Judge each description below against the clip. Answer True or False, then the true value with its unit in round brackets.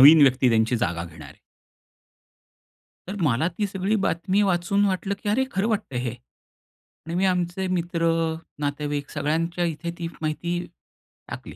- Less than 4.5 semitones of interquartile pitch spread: False (4.8 semitones)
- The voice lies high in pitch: False (170 Hz)